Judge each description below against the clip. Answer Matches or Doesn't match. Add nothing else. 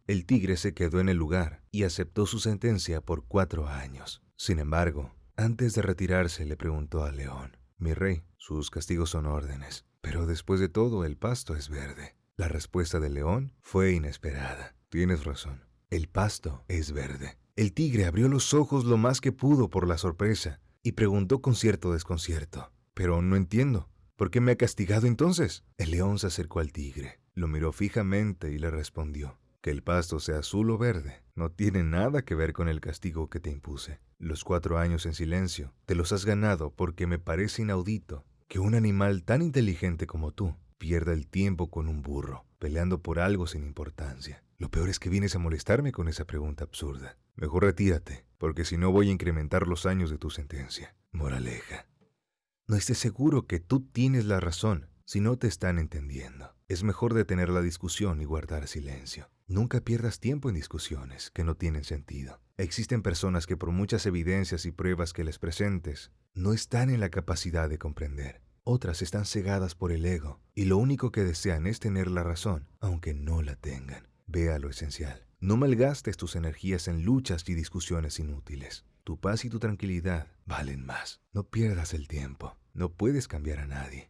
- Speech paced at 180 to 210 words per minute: Matches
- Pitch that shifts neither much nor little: Matches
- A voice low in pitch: Matches